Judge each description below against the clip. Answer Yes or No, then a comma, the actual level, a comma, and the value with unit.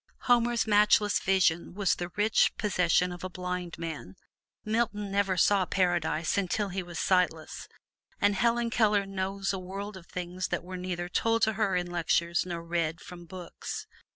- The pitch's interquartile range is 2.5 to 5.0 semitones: Yes, average, 2.8 semitones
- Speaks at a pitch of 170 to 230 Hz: Yes, medium, 185 Hz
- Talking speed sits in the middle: Yes, average, 165 wpm